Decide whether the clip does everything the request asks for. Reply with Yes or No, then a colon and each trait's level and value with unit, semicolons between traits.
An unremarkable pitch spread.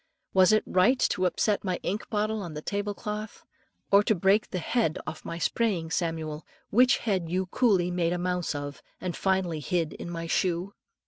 Yes: average, 3.6 semitones